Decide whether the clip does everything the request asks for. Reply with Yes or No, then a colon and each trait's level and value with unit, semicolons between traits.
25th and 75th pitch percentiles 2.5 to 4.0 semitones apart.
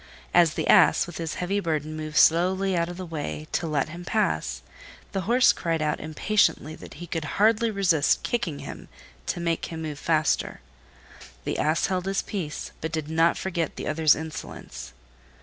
Yes: average, 3.0 semitones